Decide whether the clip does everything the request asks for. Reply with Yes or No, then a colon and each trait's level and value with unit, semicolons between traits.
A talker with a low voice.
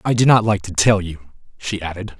Yes: low, 100 Hz